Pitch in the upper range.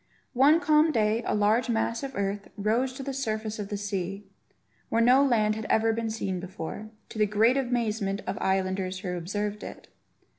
Yes: high, 215 Hz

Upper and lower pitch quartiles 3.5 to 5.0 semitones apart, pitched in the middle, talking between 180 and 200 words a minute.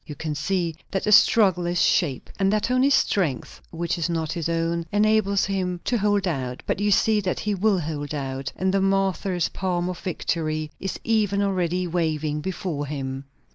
Yes: average, 3.9 semitones; medium, 180 Hz; average, 185 wpm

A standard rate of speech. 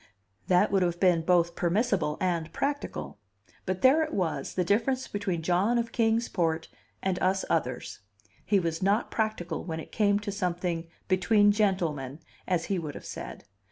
Yes: average, 165 wpm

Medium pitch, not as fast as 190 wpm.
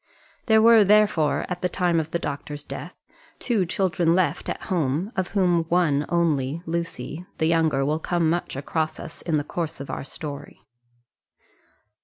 Yes: medium, 165 Hz; average, 165 wpm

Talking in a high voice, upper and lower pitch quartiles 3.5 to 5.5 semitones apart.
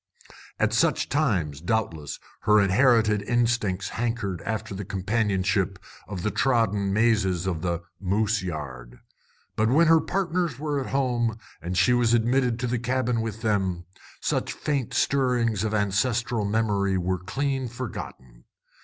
No: low, 110 Hz; average, 4.4 semitones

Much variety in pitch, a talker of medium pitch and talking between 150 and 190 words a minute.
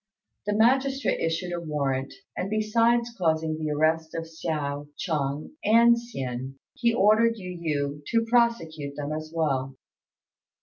No: wide, 7.5 semitones; medium, 165 Hz; slow, 135 wpm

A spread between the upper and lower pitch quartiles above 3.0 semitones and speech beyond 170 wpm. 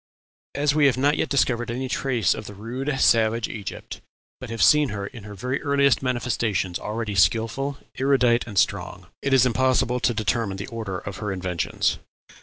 Yes: average, 4.2 semitones; average, 180 wpm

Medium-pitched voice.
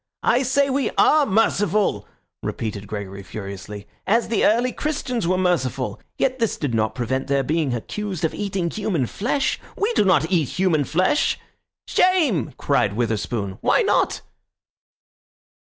Yes: medium, 170 Hz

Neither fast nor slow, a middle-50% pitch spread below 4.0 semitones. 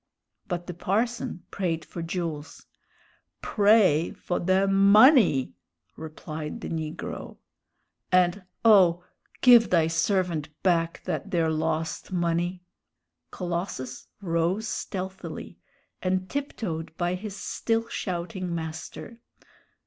No: slow, 100 wpm; average, 3.2 semitones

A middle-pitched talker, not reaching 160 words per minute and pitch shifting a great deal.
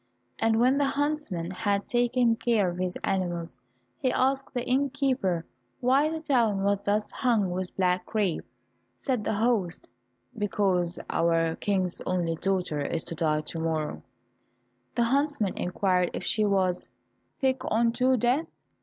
No: high, 205 Hz; average, 145 wpm; wide, 5.7 semitones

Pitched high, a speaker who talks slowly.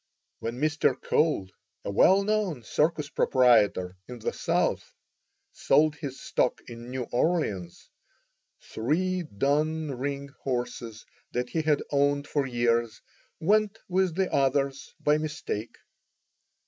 No: medium, 140 Hz; slow, 120 wpm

